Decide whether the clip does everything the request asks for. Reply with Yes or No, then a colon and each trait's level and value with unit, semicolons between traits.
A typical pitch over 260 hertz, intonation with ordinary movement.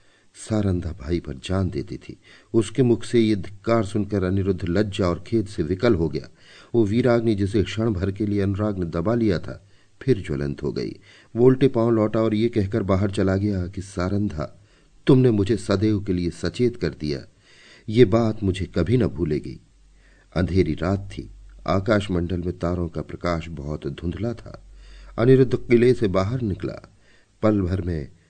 No: low, 100 Hz; average, 4.3 semitones